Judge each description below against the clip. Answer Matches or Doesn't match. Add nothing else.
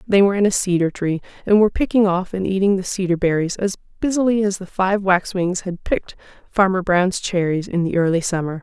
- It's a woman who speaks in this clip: Matches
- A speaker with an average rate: Doesn't match